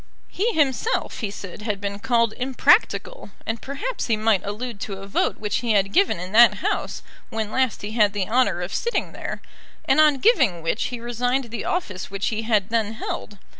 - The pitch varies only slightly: No, average, 4.1 semitones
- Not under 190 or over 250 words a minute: Yes, average, 200 wpm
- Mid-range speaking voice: No, high, 225 Hz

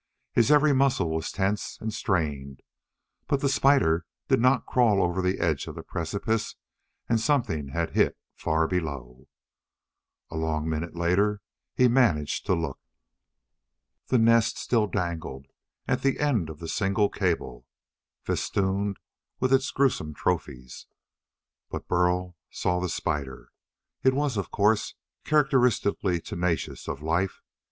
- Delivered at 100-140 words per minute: Yes, slow, 135 wpm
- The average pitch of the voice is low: Yes, very low, 95 Hz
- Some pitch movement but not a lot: No, wide, 6.4 semitones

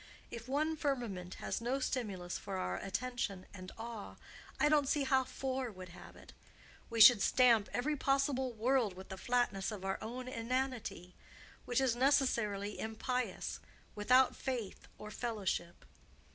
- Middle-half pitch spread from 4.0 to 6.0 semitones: Yes, average, 4.6 semitones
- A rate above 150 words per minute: No, average, 145 wpm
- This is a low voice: No, high, 235 Hz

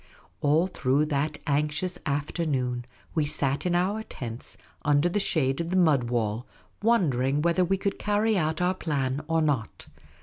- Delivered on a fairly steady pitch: No, average, 4.6 semitones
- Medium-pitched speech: Yes, medium, 150 Hz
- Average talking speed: Yes, average, 160 wpm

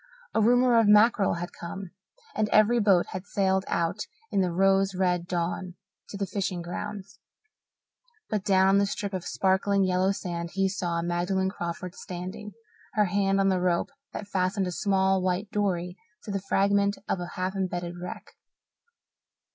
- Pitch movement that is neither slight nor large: No, narrow, 2.0 semitones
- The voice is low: No, high, 190 Hz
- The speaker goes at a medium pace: Yes, average, 165 wpm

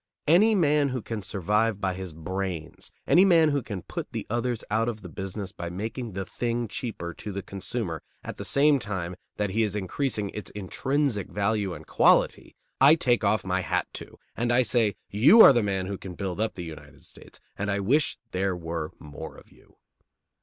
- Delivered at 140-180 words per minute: No, average, 200 wpm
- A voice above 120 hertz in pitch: No, low, 105 Hz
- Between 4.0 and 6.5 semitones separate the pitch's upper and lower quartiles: Yes, average, 4.4 semitones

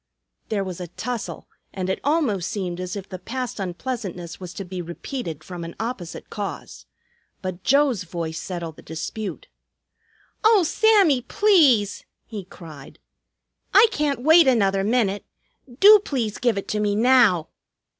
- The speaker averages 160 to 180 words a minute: No, average, 145 wpm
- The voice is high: Yes, high, 205 Hz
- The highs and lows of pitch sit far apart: Yes, wide, 6.4 semitones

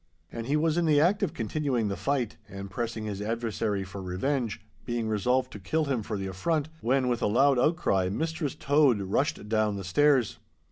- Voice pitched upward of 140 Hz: No, low, 120 Hz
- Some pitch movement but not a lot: No, wide, 6.0 semitones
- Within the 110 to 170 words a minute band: No, average, 195 wpm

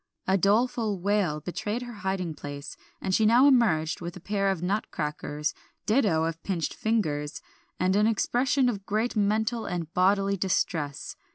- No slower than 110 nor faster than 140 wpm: No, average, 155 wpm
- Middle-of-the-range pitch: No, high, 195 Hz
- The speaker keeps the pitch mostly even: No, average, 4.6 semitones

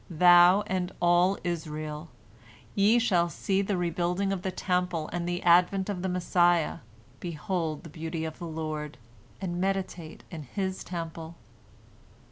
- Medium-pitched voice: Yes, medium, 175 Hz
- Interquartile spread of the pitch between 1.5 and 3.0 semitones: Yes, narrow, 2.4 semitones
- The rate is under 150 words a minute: Yes, average, 140 wpm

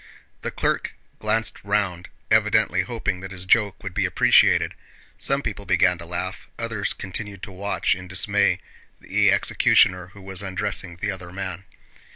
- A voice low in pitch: Yes, very low, 95 Hz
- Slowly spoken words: No, average, 155 wpm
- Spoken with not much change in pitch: Yes, narrow, 1.9 semitones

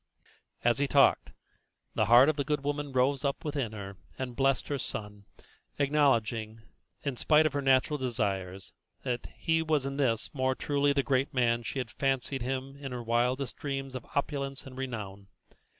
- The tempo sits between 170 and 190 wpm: Yes, average, 180 wpm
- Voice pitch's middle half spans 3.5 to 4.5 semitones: No, average, 3.0 semitones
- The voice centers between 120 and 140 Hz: Yes, low, 135 Hz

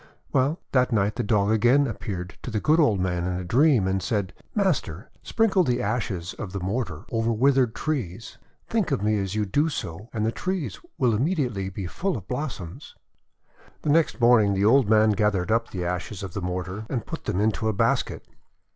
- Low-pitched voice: Yes, low, 110 Hz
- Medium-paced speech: No, fast, 210 wpm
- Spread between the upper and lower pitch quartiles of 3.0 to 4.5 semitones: No, average, 5.2 semitones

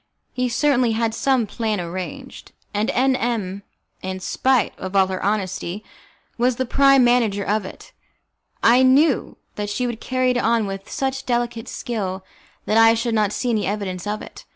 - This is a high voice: Yes, high, 225 Hz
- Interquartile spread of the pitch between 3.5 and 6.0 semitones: Yes, average, 3.8 semitones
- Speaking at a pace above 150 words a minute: Yes, average, 175 wpm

